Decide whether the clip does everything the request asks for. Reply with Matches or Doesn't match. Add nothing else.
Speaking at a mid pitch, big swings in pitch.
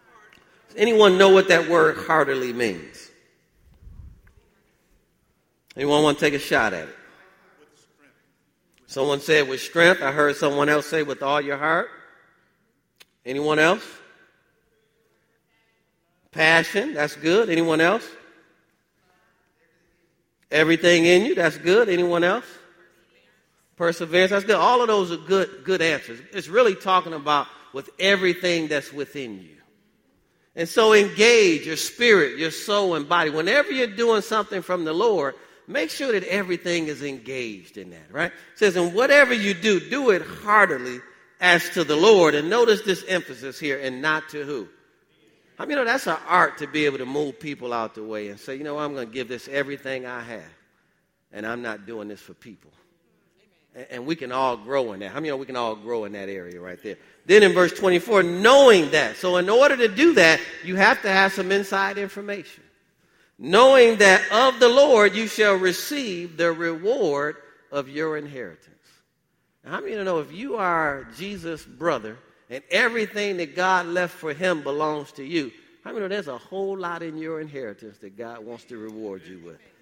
Matches